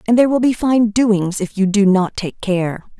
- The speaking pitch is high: Yes, high, 210 Hz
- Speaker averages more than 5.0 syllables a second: No, 4.8 syllables/s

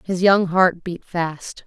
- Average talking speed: Yes, average, 180 wpm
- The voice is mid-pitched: Yes, medium, 175 Hz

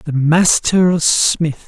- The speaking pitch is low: No, medium, 160 Hz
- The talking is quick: No, slow, 105 wpm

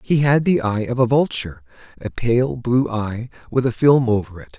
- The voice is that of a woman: No, male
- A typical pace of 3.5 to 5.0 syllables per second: Yes, 4.9 syllables/s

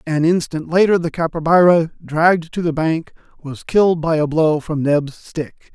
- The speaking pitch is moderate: Yes, medium, 160 Hz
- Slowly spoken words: No, average, 180 wpm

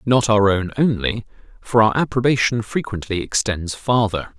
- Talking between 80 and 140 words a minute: Yes, slow, 135 wpm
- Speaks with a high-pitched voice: No, low, 110 Hz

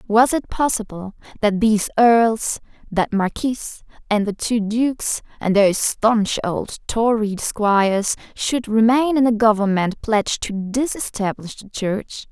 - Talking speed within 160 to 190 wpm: No, slow, 135 wpm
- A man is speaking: No, female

